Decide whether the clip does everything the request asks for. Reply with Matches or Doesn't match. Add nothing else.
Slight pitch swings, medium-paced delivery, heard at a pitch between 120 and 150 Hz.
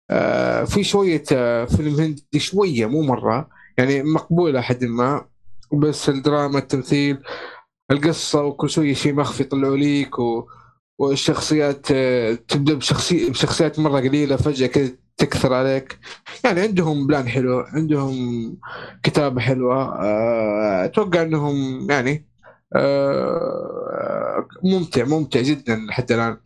Doesn't match